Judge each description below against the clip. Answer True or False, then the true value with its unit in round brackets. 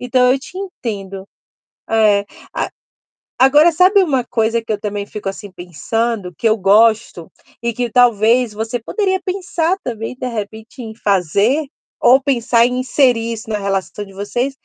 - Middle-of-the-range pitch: False (230 Hz)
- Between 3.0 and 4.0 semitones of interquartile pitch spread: True (3.6 semitones)